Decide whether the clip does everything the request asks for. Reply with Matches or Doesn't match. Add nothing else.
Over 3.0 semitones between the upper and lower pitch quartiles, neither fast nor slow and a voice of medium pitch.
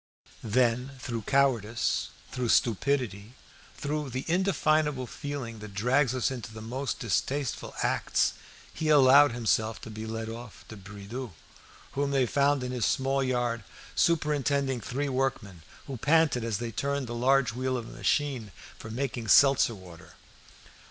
Doesn't match